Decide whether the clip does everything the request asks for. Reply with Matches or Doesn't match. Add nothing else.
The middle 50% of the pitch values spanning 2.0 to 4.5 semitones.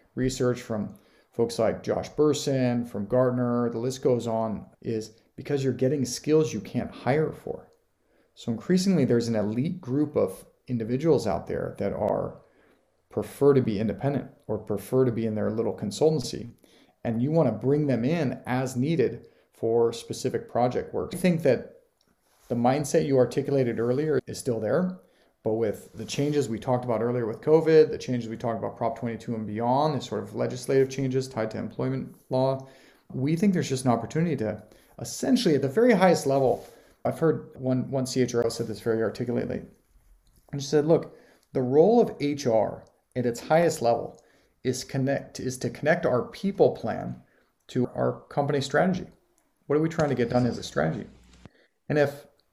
Matches